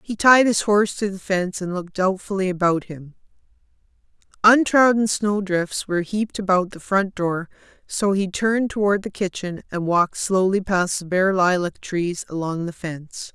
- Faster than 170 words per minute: No, average, 165 wpm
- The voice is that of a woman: Yes, female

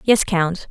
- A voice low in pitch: No, medium, 185 Hz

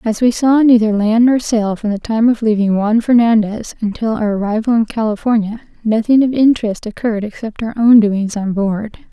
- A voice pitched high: Yes, high, 220 Hz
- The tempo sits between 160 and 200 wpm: Yes, average, 190 wpm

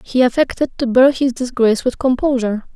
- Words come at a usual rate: Yes, average, 175 wpm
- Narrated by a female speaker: Yes, female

